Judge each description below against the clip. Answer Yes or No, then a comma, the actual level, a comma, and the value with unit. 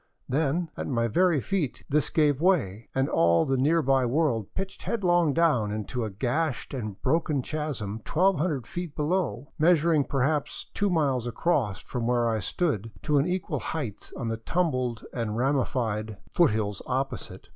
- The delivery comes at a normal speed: Yes, average, 155 wpm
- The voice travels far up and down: Yes, wide, 5.8 semitones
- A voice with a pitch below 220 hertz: Yes, low, 135 Hz